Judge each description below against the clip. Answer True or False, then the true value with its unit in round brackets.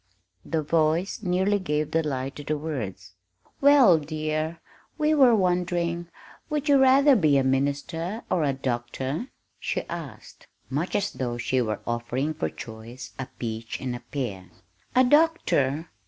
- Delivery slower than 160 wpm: True (150 wpm)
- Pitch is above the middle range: False (155 Hz)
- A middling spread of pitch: False (5.9 semitones)